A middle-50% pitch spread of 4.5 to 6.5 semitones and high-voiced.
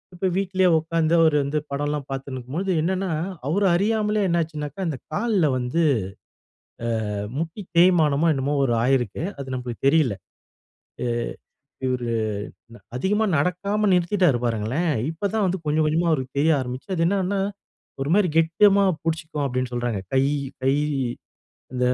No: wide, 5.5 semitones; medium, 160 Hz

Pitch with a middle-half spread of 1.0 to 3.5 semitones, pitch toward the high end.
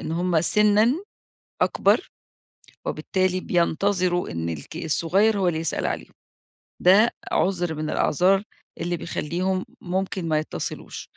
No: average, 2.9 semitones; medium, 180 Hz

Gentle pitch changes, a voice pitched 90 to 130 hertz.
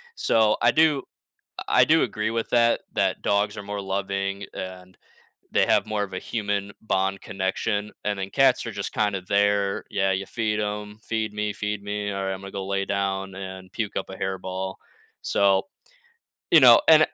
Yes: narrow, 1.6 semitones; low, 100 Hz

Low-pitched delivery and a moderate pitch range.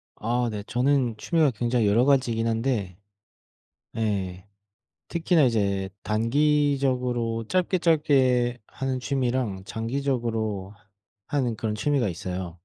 Yes: low, 120 Hz; average, 4.1 semitones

